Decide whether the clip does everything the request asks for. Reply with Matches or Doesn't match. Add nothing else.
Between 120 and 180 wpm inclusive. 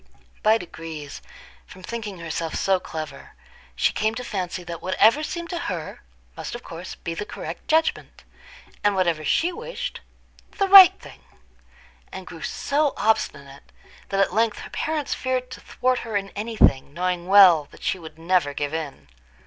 Matches